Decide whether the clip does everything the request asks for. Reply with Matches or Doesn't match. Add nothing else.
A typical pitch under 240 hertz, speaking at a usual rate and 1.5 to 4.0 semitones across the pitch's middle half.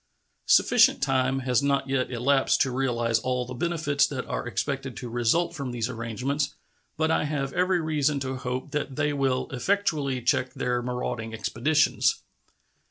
Matches